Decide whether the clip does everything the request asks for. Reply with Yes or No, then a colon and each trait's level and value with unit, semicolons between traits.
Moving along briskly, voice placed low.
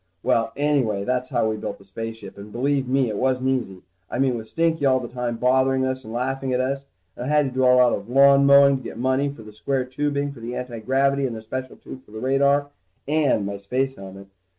Yes: fast, 240 wpm; low, 130 Hz